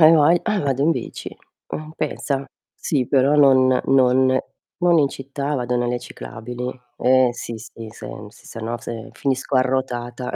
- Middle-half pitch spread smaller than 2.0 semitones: No, narrow, 2.4 semitones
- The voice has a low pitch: Yes, low, 130 Hz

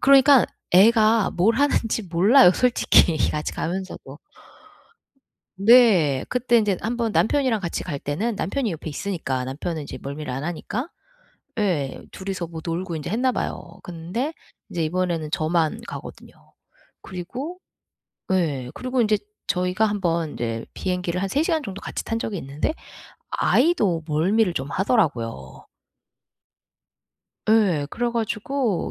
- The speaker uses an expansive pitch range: Yes, wide, 6.0 semitones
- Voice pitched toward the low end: No, medium, 185 Hz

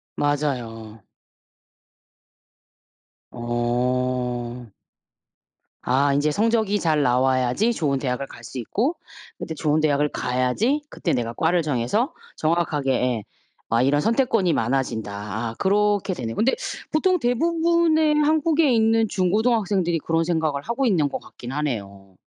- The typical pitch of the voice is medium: Yes, medium, 150 Hz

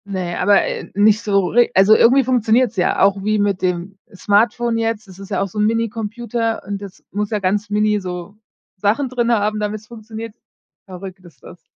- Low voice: No, high, 210 Hz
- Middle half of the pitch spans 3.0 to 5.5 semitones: No, narrow, 2.6 semitones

